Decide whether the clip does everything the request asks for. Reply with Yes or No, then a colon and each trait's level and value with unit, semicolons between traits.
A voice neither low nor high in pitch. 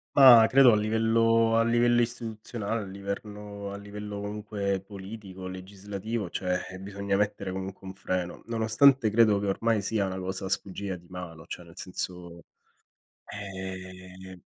No: low, 100 Hz